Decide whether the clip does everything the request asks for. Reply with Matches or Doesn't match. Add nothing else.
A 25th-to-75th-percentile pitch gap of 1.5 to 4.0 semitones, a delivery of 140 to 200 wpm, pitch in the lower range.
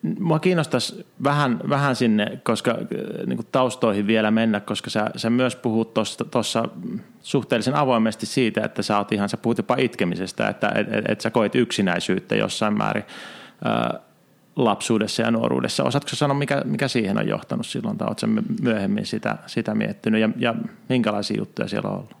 Doesn't match